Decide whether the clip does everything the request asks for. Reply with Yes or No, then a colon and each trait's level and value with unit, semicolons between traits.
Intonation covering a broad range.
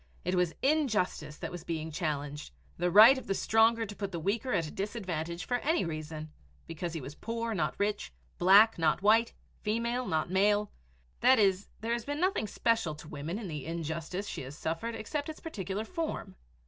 Yes: wide, 6.0 semitones